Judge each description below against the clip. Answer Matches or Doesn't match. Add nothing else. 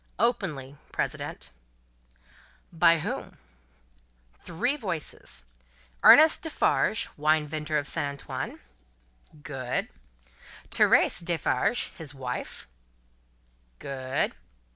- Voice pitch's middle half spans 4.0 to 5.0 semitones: Matches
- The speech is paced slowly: Matches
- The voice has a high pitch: Doesn't match